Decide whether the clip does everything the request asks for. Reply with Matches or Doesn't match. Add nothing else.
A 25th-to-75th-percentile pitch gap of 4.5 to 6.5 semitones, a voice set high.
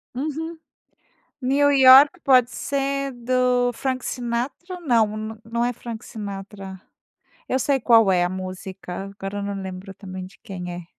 Matches